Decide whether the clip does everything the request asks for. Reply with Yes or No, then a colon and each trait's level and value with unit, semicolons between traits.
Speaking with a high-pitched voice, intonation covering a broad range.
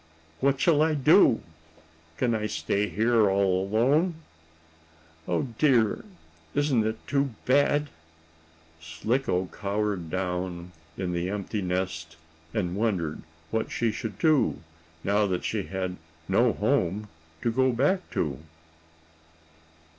No: low, 105 Hz; wide, 6.0 semitones